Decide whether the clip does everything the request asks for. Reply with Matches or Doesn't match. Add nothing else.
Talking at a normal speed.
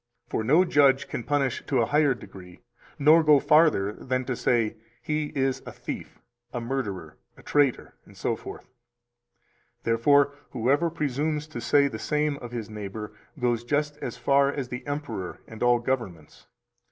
Matches